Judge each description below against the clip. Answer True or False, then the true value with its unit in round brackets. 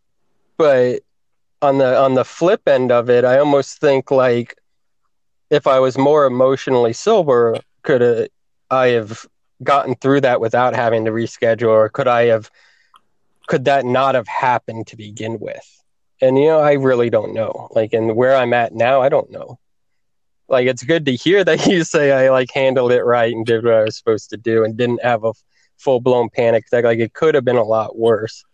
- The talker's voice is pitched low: True (125 Hz)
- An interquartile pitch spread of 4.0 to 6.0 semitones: False (3.1 semitones)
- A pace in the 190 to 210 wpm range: True (200 wpm)